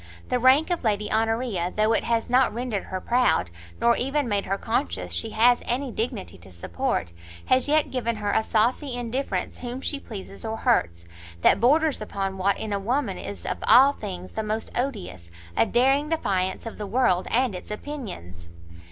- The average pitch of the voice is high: Yes, high, 225 Hz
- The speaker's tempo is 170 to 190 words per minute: Yes, average, 185 wpm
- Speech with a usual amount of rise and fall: Yes, average, 4.8 semitones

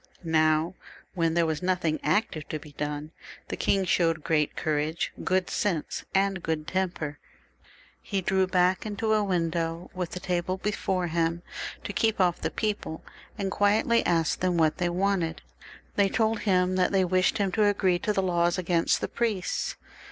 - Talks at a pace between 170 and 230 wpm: Yes, average, 175 wpm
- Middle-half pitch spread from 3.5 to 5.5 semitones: No, average, 2.9 semitones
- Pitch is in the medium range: Yes, medium, 180 Hz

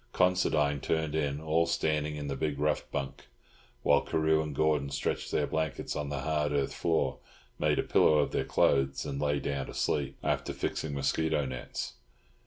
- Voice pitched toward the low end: Yes, very low, 75 Hz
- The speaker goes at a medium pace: Yes, average, 180 wpm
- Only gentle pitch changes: Yes, narrow, 2.0 semitones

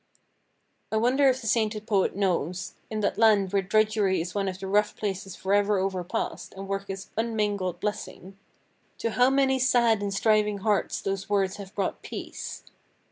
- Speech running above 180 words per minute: No, average, 160 wpm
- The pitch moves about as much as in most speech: No, narrow, 2.1 semitones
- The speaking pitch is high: Yes, high, 205 Hz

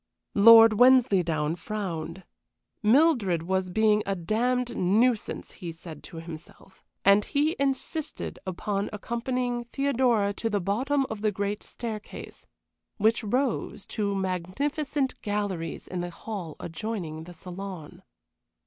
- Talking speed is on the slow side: Yes, slow, 120 wpm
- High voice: Yes, high, 205 Hz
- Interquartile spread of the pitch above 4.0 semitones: Yes, average, 5.1 semitones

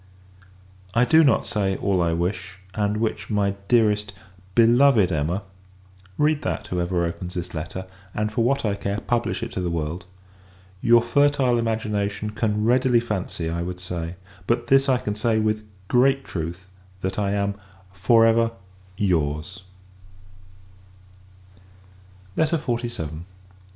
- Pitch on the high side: No, low, 105 Hz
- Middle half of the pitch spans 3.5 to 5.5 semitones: Yes, average, 4.6 semitones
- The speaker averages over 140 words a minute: No, slow, 135 wpm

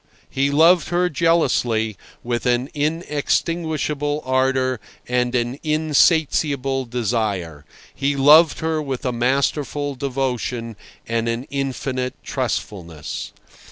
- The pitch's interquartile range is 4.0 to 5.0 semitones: No, average, 3.6 semitones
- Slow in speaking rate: Yes, slow, 95 wpm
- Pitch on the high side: No, low, 135 Hz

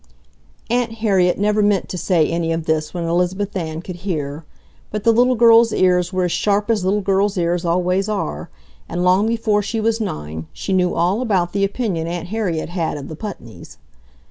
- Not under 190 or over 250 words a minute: Yes, average, 195 wpm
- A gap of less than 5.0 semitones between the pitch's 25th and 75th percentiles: Yes, average, 3.6 semitones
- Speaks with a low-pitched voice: No, medium, 185 Hz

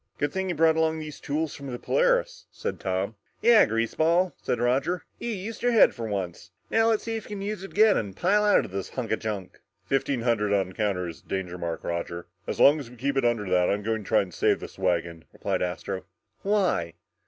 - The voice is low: Yes, low, 125 Hz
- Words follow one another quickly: Yes, fast, 235 wpm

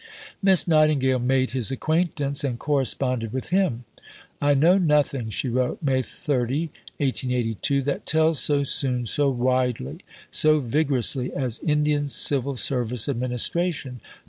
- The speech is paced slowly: Yes, slow, 125 wpm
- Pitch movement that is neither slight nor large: Yes, average, 3.1 semitones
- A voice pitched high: No, low, 135 Hz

